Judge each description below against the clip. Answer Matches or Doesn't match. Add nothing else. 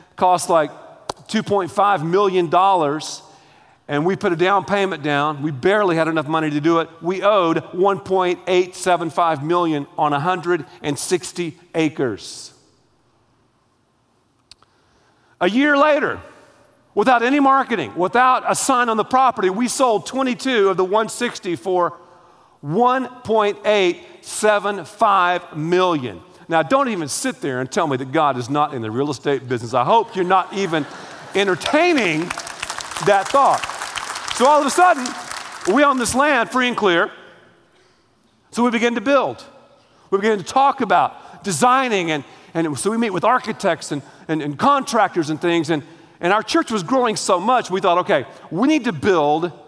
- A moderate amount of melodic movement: Doesn't match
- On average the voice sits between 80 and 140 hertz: Doesn't match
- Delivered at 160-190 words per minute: Doesn't match